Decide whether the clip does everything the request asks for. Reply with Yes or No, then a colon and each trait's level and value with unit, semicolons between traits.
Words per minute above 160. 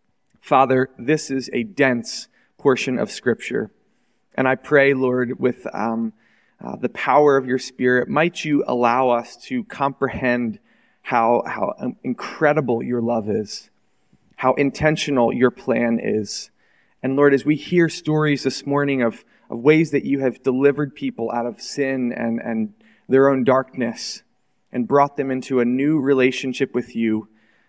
No: average, 150 wpm